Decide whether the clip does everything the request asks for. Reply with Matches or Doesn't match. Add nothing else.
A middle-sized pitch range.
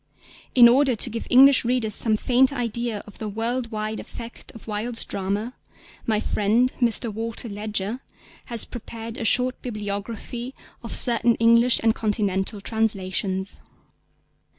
Doesn't match